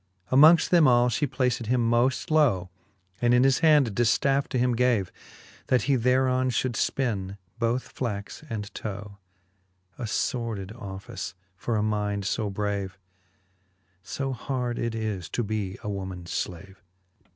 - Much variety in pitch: No, average, 4.1 semitones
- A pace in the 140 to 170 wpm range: Yes, average, 150 wpm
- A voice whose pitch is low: Yes, low, 115 Hz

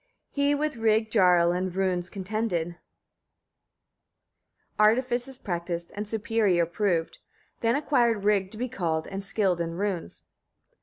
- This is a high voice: Yes, high, 200 Hz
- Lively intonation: No, average, 4.4 semitones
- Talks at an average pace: No, slow, 125 wpm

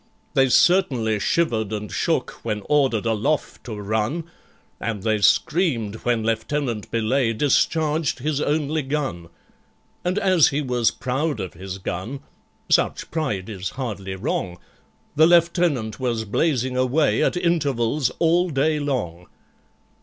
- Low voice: Yes, low, 130 Hz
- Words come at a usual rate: No, slow, 125 wpm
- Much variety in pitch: Yes, wide, 5.9 semitones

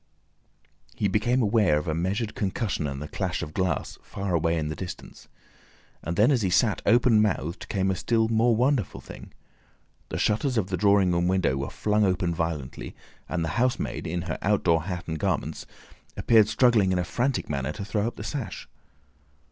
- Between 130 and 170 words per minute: No, average, 190 wpm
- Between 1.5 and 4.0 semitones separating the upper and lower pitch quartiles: No, average, 4.7 semitones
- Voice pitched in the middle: No, very low, 95 Hz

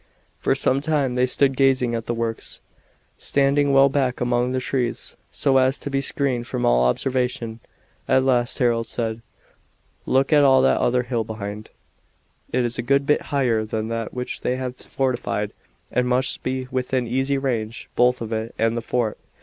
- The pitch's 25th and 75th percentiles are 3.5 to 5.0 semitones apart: No, narrow, 2.5 semitones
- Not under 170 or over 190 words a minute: Yes, average, 175 wpm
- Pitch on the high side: No, low, 125 Hz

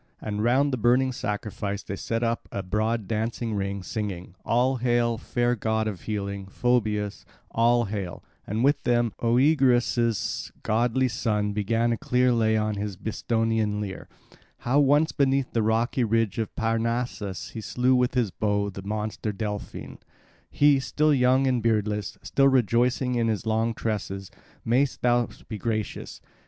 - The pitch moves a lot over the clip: No, average, 2.7 semitones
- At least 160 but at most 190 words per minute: No, average, 150 wpm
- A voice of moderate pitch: No, low, 115 Hz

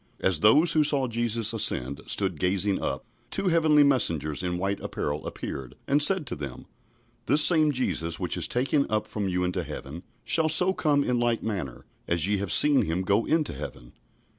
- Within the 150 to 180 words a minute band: No, average, 190 wpm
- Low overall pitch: Yes, low, 105 Hz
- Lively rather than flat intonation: Yes, wide, 9.0 semitones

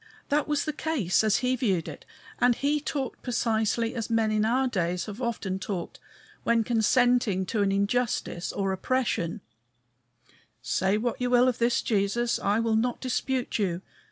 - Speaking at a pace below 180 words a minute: Yes, average, 165 wpm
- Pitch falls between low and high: No, high, 230 Hz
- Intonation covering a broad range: No, average, 3.8 semitones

